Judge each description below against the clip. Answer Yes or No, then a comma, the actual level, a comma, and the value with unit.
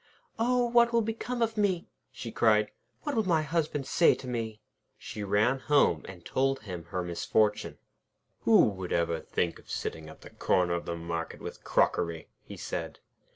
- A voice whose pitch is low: Yes, low, 110 Hz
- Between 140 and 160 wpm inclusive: No, average, 175 wpm